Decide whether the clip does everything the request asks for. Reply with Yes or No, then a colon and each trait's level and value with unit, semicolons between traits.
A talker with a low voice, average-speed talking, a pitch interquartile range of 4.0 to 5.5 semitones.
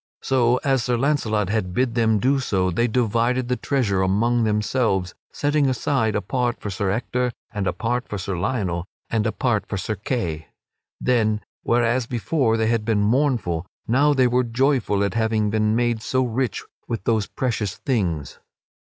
No: low, 115 Hz; average, 175 wpm; average, 3.4 semitones